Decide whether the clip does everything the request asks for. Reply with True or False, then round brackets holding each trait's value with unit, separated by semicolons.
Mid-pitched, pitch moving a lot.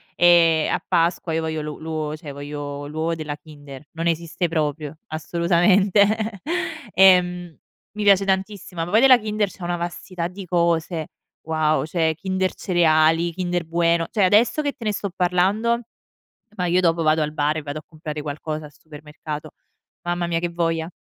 False (170 Hz; 2.8 semitones)